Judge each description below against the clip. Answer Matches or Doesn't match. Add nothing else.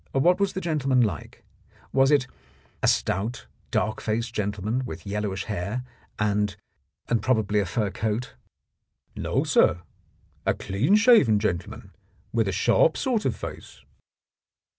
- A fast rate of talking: Doesn't match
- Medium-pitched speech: Doesn't match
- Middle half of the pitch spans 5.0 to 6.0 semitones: Doesn't match